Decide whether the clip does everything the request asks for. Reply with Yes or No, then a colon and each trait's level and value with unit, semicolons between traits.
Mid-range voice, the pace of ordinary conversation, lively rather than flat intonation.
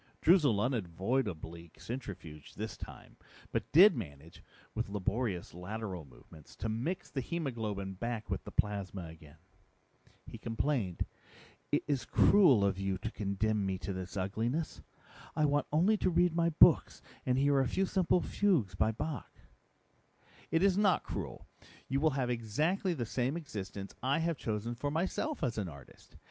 No: low, 115 Hz; average, 155 wpm; wide, 7.7 semitones